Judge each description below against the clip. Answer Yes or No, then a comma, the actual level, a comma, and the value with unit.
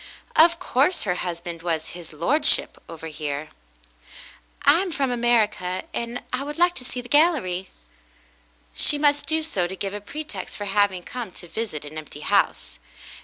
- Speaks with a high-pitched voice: Yes, high, 210 Hz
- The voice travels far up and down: Yes, wide, 8.7 semitones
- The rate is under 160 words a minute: No, average, 170 wpm